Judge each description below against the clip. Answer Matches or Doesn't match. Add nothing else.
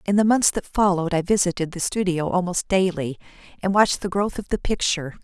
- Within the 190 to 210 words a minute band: Matches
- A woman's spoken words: Matches